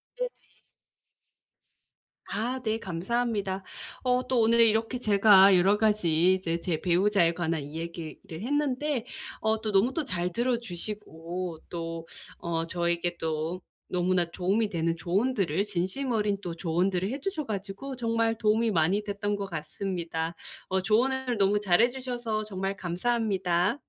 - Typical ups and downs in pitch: Yes, average, 4.8 semitones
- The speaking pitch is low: No, high, 195 Hz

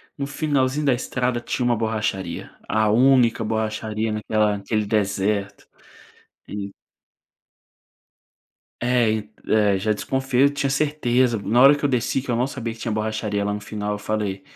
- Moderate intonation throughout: Yes, average, 3.3 semitones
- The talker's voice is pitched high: No, low, 110 Hz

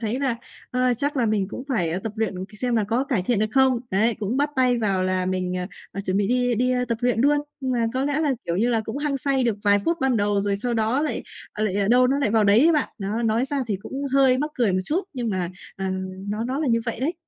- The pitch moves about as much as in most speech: Yes, average, 4.3 semitones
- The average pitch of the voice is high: Yes, high, 230 Hz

